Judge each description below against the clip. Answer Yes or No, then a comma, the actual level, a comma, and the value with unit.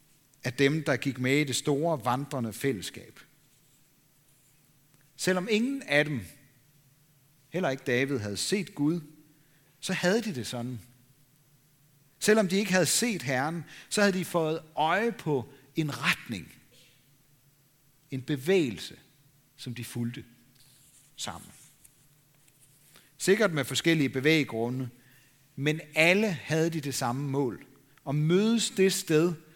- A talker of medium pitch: Yes, medium, 145 Hz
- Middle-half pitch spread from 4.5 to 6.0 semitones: No, narrow, 2.6 semitones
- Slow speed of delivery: Yes, slow, 120 wpm